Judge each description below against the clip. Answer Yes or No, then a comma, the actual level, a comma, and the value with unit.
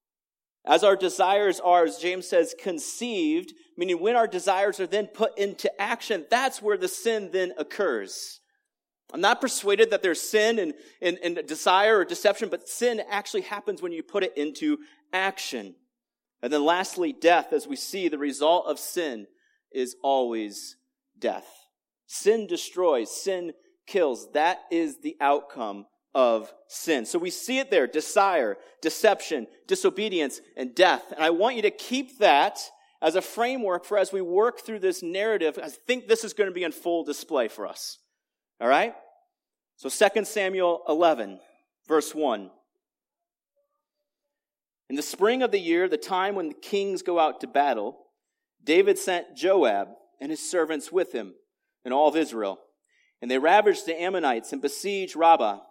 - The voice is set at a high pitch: Yes, high, 220 Hz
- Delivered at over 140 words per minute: Yes, average, 165 wpm